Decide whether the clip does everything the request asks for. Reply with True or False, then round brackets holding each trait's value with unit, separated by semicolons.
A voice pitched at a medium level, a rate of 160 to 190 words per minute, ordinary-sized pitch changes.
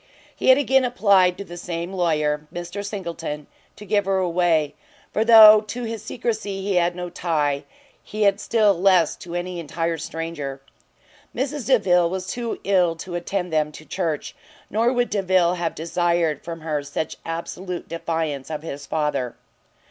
True (175 Hz; 165 wpm; 3.7 semitones)